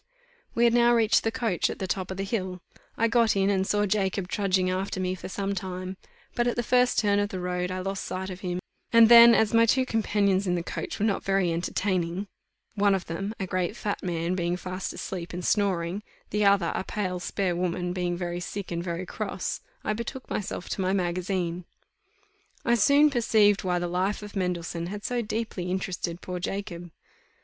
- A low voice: No, high, 190 Hz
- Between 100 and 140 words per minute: No, fast, 205 wpm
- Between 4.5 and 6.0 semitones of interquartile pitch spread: No, narrow, 2.6 semitones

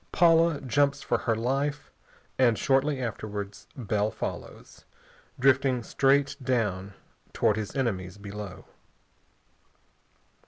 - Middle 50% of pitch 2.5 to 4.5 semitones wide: No, average, 5.1 semitones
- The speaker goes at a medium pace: No, slow, 95 wpm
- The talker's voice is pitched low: Yes, low, 125 Hz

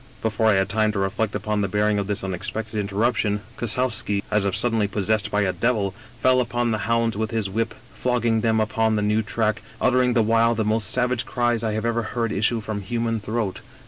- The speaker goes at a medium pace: No, fast, 225 wpm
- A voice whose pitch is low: Yes, low, 110 Hz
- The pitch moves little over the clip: Yes, narrow, 2.0 semitones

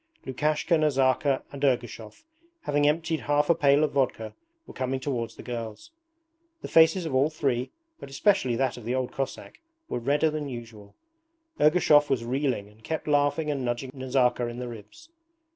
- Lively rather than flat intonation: No, average, 3.5 semitones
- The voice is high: No, low, 135 Hz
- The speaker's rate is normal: Yes, average, 170 wpm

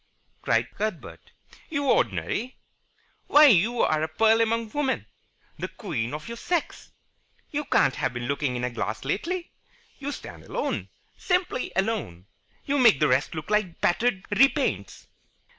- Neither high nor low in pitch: No, high, 215 Hz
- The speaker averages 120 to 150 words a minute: Yes, average, 145 wpm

